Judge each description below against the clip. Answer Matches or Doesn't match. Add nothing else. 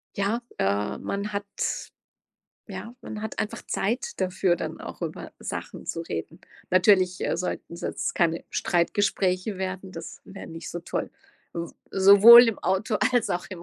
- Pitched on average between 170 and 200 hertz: Matches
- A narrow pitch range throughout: Doesn't match